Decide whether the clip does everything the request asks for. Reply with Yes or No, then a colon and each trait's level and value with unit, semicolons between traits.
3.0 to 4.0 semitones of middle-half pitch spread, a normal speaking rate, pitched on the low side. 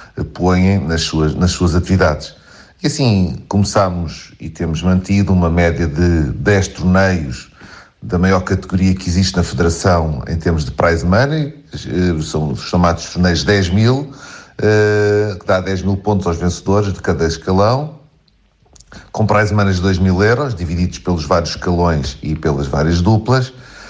Yes: average, 3.3 semitones; average, 155 wpm; very low, 95 Hz